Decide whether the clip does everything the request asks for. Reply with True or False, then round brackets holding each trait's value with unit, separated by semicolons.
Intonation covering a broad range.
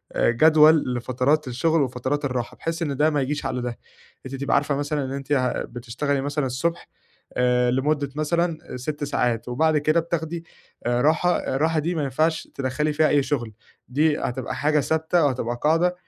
False (3.5 semitones)